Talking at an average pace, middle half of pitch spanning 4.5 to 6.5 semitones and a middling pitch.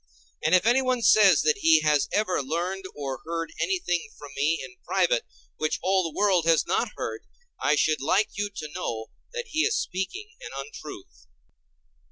Yes: average, 175 wpm; average, 5.2 semitones; medium, 170 Hz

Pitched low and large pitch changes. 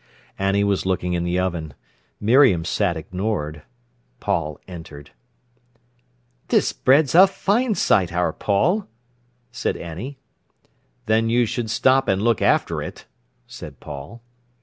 Yes: low, 100 Hz; wide, 5.8 semitones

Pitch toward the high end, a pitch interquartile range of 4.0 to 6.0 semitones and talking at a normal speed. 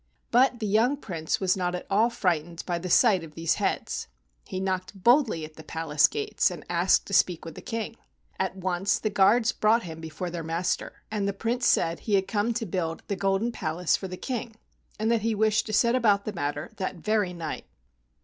No: high, 195 Hz; average, 4.5 semitones; fast, 215 wpm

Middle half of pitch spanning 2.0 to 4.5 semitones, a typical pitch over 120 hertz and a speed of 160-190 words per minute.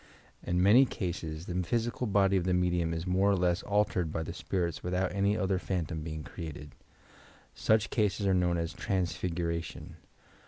No: average, 2.8 semitones; very low, 90 Hz; average, 165 wpm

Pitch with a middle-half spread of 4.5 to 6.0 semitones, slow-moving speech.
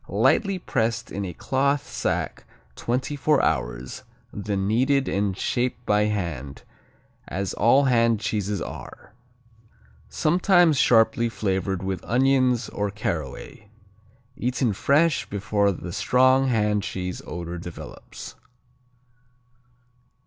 Yes: average, 5.3 semitones; slow, 105 wpm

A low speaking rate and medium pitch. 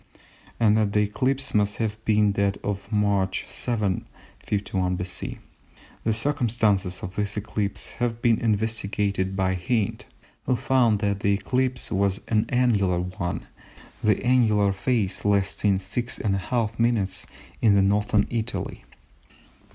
No: slow, 125 wpm; low, 105 Hz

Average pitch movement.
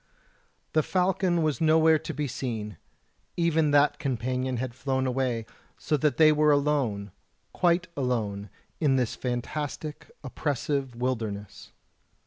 Yes: average, 4.0 semitones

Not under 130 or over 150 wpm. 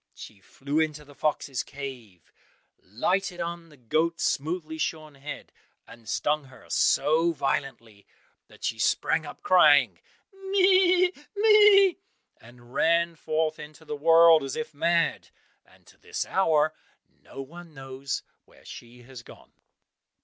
Yes: slow, 135 wpm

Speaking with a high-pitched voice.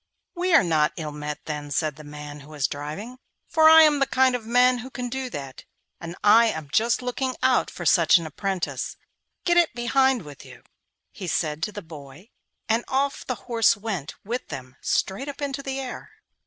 Yes: high, 220 Hz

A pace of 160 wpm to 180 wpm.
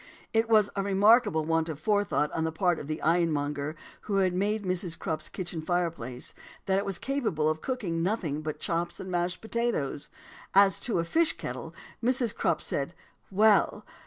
Yes: average, 175 wpm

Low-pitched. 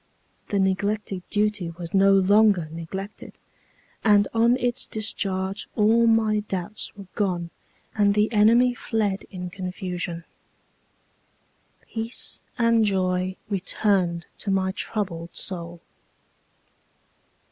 No: high, 200 Hz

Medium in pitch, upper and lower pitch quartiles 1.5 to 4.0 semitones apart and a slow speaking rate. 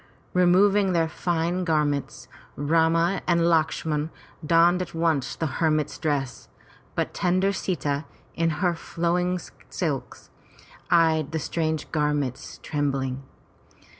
Yes: medium, 165 Hz; average, 2.8 semitones; slow, 115 wpm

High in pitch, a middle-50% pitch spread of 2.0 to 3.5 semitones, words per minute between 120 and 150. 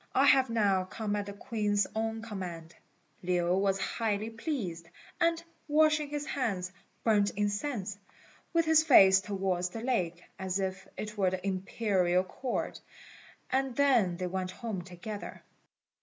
No: high, 205 Hz; average, 4.2 semitones; average, 140 wpm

